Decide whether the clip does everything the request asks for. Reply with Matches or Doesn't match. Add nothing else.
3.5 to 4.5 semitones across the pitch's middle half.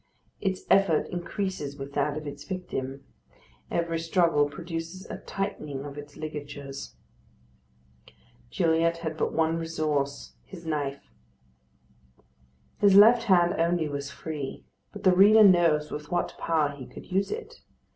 Matches